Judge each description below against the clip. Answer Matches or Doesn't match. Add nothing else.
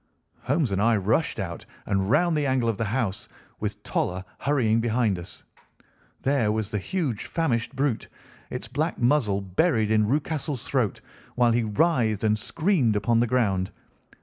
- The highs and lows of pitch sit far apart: Doesn't match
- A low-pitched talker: Matches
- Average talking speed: Matches